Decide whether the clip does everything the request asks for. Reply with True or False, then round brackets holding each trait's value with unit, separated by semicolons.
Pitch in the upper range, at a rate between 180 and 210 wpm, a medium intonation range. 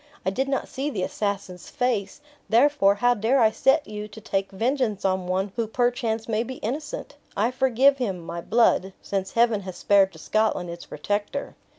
True (220 Hz; 185 wpm; 4.2 semitones)